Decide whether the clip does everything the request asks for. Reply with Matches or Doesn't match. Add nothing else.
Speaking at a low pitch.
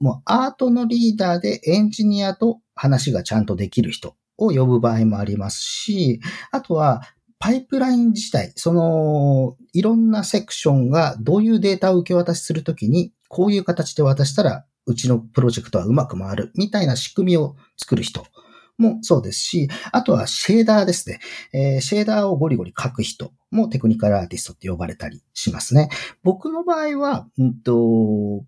Doesn't match